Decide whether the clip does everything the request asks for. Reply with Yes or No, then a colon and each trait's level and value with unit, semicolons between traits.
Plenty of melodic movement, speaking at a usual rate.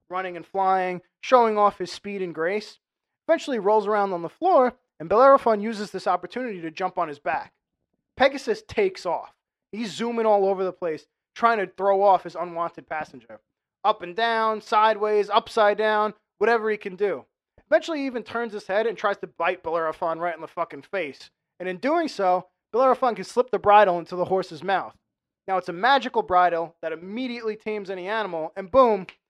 No: average, 4.1 semitones; average, 190 wpm